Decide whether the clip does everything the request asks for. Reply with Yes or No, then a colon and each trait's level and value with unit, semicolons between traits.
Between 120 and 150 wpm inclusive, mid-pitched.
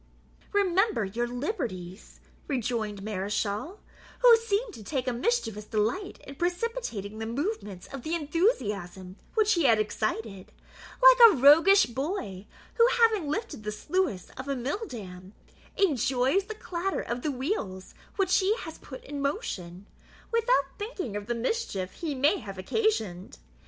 No: average, 145 wpm; very high, 270 Hz